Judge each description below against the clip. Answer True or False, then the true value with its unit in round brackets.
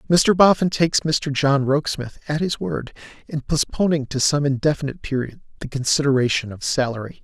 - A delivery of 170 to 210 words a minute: False (160 wpm)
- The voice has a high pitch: False (145 Hz)